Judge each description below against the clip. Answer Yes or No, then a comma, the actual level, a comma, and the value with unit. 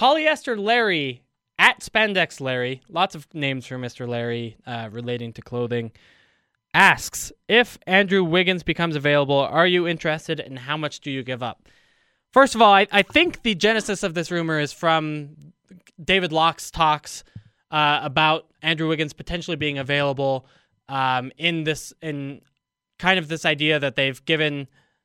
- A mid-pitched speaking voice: Yes, medium, 155 Hz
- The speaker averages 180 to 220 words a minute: No, average, 155 wpm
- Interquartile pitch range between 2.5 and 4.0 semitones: No, average, 5.0 semitones